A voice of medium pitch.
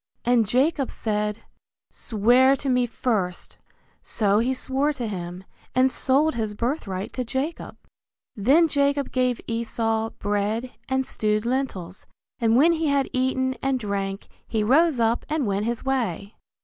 No: high, 240 Hz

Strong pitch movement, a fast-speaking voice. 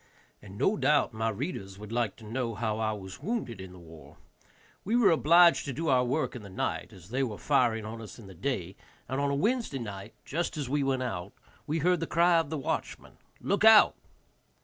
Yes: wide, 6.9 semitones; fast, 220 wpm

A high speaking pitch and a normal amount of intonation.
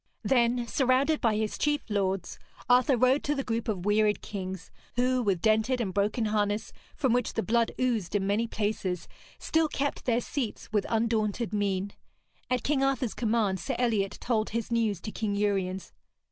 Yes: high, 220 Hz; average, 3.4 semitones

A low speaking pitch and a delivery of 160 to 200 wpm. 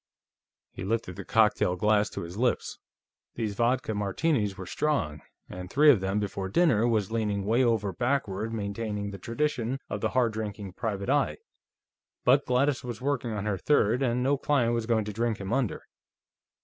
Yes: low, 110 Hz; average, 175 wpm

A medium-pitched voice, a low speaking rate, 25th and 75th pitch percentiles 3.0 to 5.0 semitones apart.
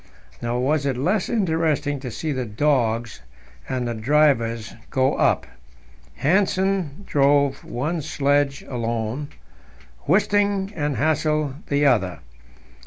Yes: medium, 145 Hz; slow, 110 wpm; average, 4.3 semitones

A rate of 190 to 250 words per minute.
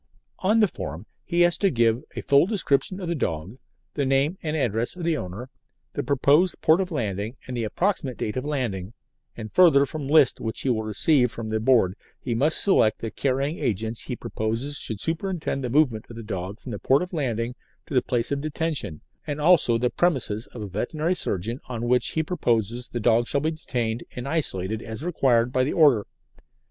Yes: fast, 205 wpm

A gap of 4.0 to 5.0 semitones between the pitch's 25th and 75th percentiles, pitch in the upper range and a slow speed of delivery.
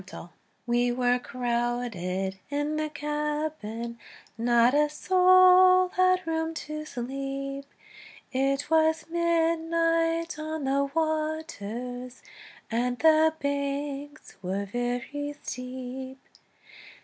Yes: average, 4.4 semitones; very high, 285 Hz; slow, 90 wpm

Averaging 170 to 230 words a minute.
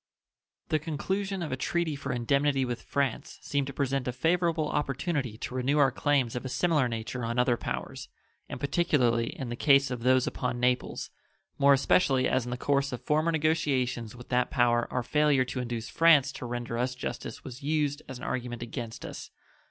Yes: average, 190 wpm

